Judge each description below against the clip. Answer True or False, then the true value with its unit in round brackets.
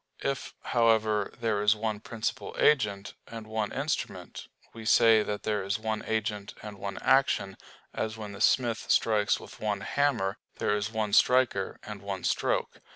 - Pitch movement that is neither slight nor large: False (1.8 semitones)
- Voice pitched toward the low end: True (110 Hz)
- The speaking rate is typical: True (160 wpm)